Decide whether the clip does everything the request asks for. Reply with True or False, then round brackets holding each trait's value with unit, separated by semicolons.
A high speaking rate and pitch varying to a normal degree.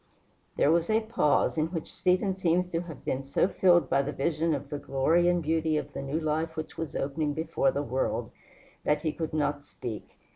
True (210 wpm; 3.1 semitones)